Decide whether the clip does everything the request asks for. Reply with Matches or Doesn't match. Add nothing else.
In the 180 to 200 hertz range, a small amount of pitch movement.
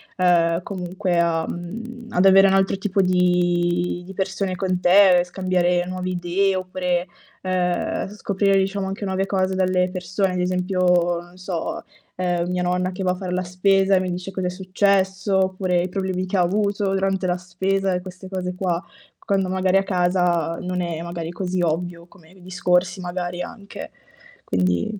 Matches